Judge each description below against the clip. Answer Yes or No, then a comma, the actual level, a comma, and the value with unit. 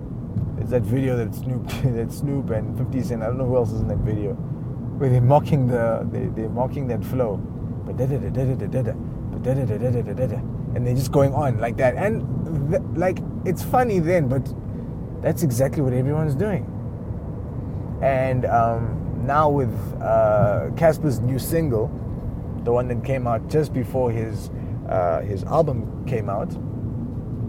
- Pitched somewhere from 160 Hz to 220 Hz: No, low, 125 Hz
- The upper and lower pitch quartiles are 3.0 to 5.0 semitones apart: No, narrow, 2.6 semitones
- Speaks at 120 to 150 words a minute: Yes, average, 140 wpm